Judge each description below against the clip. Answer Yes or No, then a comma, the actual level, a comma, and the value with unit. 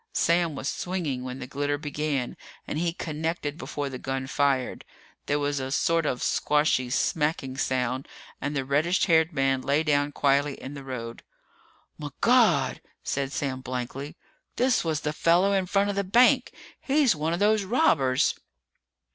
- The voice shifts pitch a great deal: No, average, 4.0 semitones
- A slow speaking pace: No, average, 160 wpm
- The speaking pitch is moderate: Yes, medium, 145 Hz